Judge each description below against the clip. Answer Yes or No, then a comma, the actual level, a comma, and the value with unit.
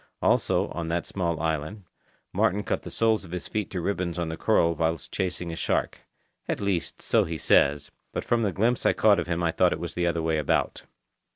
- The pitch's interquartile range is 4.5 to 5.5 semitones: No, average, 3.2 semitones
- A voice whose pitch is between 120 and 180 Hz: No, very low, 85 Hz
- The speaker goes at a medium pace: No, fast, 215 wpm